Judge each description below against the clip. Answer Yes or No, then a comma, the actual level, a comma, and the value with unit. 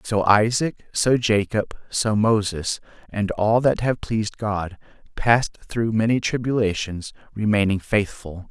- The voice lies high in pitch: No, low, 105 Hz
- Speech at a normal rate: No, slow, 125 wpm